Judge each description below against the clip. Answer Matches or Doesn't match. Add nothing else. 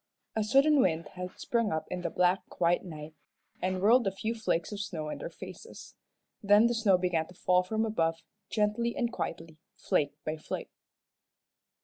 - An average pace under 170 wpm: Doesn't match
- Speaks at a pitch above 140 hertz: Matches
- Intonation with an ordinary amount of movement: Matches